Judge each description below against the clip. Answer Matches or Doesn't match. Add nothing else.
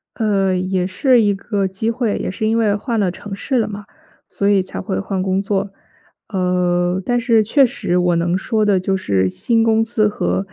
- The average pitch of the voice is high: Matches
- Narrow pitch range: Doesn't match